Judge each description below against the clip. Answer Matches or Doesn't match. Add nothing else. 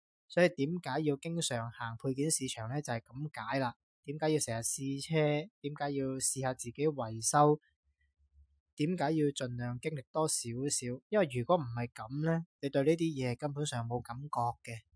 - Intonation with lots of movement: Doesn't match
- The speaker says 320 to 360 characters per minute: Doesn't match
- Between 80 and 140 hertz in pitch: Matches